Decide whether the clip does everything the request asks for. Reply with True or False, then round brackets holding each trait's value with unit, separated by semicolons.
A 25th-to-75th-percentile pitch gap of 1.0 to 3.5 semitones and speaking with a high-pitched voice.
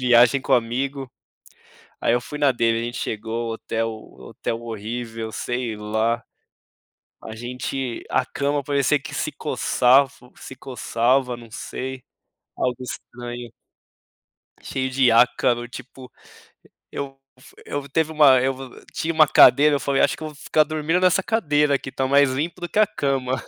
False (3.0 semitones; 130 Hz)